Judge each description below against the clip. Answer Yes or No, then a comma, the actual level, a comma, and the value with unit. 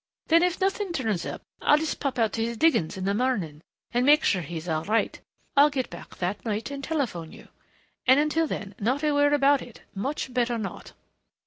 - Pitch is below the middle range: No, very high, 250 Hz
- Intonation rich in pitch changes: Yes, wide, 6.4 semitones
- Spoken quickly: Yes, fast, 210 wpm